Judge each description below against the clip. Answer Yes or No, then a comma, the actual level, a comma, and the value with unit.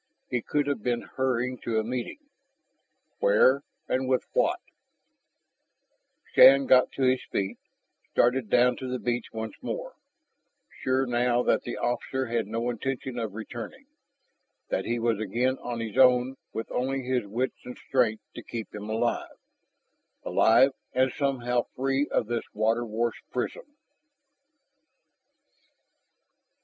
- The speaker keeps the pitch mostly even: Yes, narrow, 2.1 semitones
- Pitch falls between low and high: No, low, 125 Hz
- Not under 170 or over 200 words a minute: No, slow, 135 wpm